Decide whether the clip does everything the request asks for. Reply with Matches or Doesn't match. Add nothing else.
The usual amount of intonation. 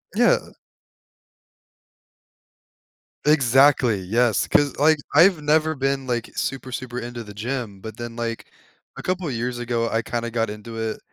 Matches